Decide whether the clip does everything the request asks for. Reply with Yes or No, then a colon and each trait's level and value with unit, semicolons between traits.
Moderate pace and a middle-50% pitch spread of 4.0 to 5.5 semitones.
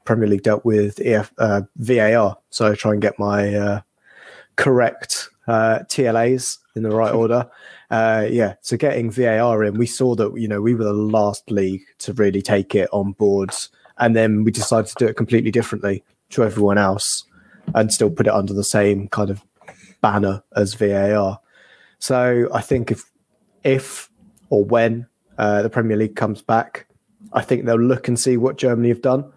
No: average, 185 wpm; narrow, 2.5 semitones